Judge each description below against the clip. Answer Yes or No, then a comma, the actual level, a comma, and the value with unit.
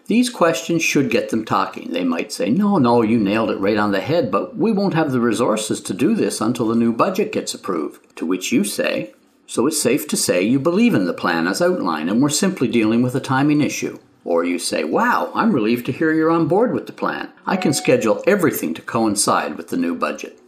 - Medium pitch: Yes, medium, 150 Hz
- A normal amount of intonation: No, wide, 8.9 semitones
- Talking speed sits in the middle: No, fast, 235 wpm